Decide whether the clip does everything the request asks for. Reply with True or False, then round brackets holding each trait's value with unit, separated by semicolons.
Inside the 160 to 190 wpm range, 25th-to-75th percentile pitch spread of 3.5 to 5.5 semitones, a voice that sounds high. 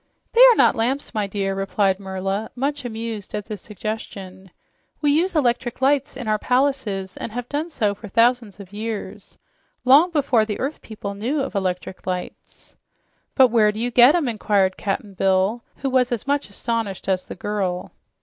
True (180 wpm; 4.6 semitones; 220 Hz)